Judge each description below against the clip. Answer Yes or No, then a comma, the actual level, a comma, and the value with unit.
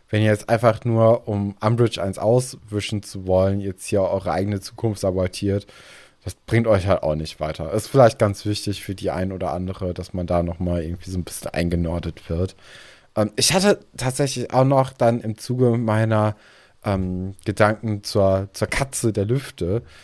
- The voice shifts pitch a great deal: No, average, 3.6 semitones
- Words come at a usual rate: Yes, average, 180 wpm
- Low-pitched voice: Yes, low, 105 Hz